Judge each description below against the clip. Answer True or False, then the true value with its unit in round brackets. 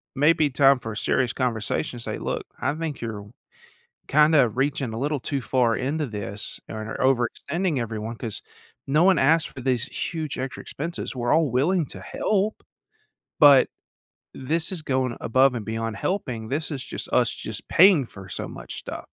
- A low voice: True (130 Hz)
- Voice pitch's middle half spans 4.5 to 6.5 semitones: True (4.8 semitones)